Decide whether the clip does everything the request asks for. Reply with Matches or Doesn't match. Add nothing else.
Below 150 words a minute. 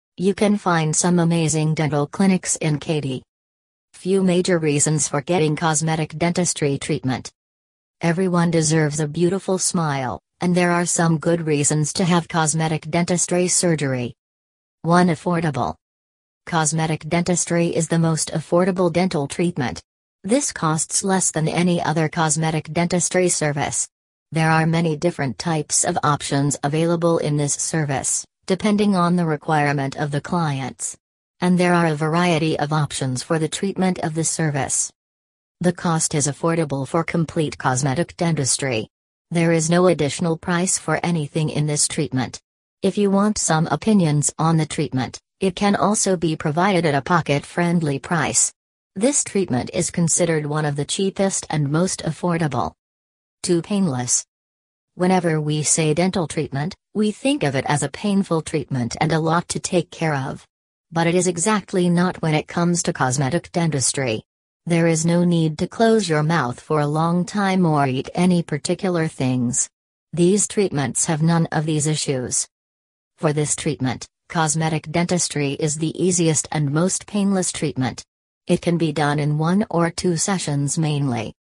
Doesn't match